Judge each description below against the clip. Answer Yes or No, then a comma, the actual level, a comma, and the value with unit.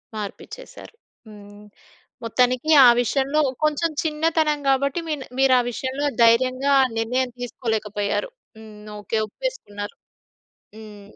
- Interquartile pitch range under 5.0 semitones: No, average, 5.3 semitones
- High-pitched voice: Yes, very high, 255 Hz